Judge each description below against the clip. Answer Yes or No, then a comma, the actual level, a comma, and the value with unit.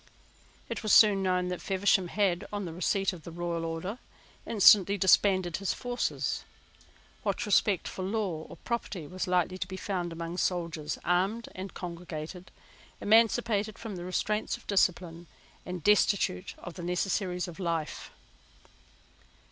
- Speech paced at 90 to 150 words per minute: Yes, average, 145 wpm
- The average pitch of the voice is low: No, medium, 185 Hz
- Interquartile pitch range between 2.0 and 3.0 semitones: Yes, narrow, 2.6 semitones